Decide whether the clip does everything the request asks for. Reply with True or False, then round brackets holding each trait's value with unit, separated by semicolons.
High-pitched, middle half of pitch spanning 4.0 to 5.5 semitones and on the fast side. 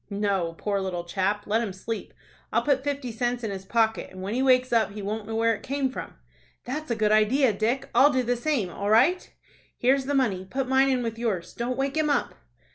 True (230 Hz; 4.4 semitones; 230 wpm)